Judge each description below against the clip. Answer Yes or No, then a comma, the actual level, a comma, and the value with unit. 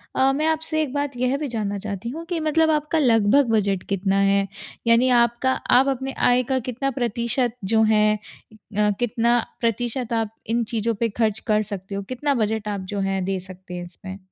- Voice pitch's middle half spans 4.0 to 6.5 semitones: Yes, average, 4.4 semitones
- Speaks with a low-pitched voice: No, high, 230 Hz